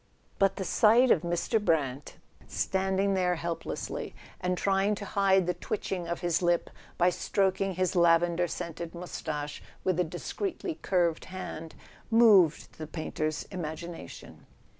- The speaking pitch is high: No, medium, 180 Hz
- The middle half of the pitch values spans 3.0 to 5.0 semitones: No, narrow, 2.4 semitones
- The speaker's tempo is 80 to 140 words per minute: Yes, slow, 135 wpm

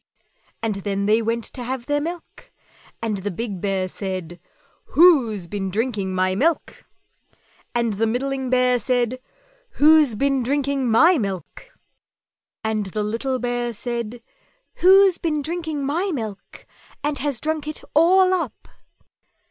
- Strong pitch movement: Yes, wide, 5.7 semitones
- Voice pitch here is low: No, high, 245 Hz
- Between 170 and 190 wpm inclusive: No, average, 140 wpm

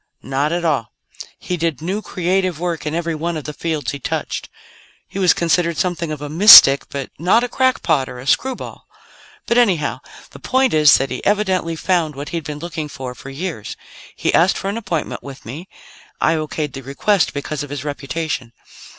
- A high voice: No, medium, 160 Hz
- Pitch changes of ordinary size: Yes, average, 4.0 semitones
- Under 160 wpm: No, average, 195 wpm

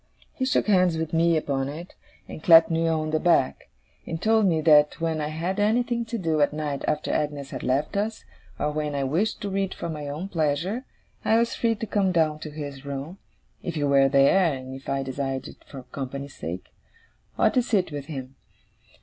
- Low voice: No, medium, 155 Hz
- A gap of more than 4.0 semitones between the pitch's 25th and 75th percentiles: Yes, average, 4.7 semitones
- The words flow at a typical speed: No, fast, 210 wpm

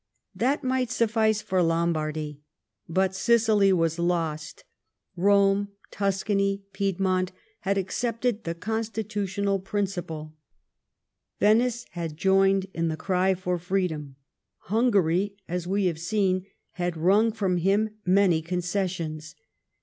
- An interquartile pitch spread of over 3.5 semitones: No, average, 3.1 semitones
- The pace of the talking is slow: Yes, slow, 105 wpm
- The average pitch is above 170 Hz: Yes, high, 190 Hz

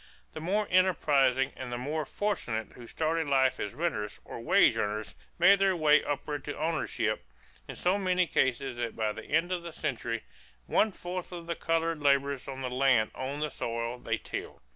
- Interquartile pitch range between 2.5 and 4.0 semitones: No, average, 5.3 semitones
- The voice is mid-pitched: Yes, medium, 145 Hz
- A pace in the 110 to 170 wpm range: No, average, 185 wpm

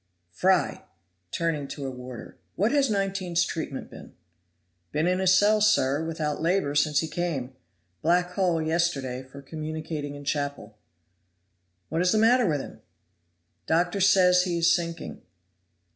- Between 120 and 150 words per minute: Yes, average, 140 wpm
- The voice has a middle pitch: Yes, medium, 165 Hz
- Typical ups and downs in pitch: Yes, average, 4.1 semitones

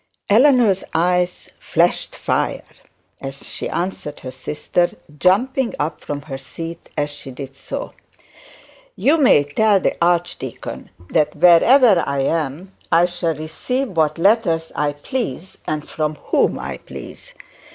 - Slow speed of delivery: Yes, slow, 130 wpm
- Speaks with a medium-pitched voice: Yes, medium, 170 Hz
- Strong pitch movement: No, average, 4.7 semitones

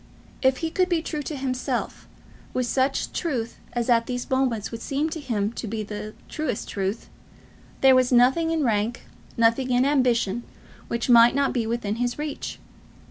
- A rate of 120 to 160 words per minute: No, average, 175 wpm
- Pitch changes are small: No, average, 3.1 semitones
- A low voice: No, high, 245 Hz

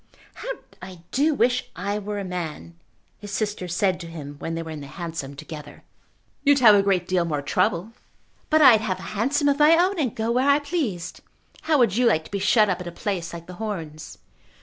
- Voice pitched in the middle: No, high, 195 Hz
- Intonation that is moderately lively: No, wide, 6.3 semitones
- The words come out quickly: Yes, fast, 220 wpm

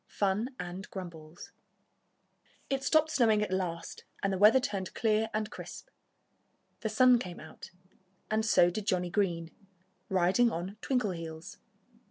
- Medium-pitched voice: No, high, 195 Hz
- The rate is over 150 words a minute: No, average, 140 wpm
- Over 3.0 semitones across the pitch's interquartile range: Yes, average, 3.9 semitones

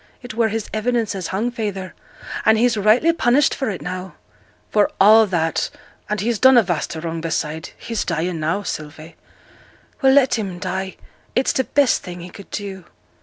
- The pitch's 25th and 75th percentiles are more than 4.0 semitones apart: Yes, average, 4.9 semitones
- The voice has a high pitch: Yes, high, 205 Hz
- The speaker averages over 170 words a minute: Yes, average, 180 wpm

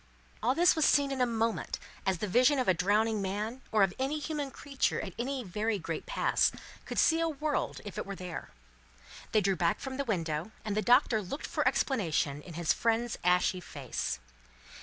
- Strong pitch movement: Yes, wide, 6.4 semitones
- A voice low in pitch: No, high, 220 Hz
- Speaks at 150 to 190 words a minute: No, average, 200 wpm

